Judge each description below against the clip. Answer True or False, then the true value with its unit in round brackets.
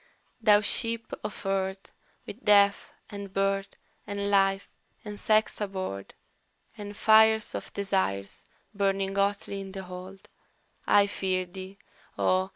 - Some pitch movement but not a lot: False (1.2 semitones)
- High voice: True (195 Hz)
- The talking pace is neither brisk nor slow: False (125 wpm)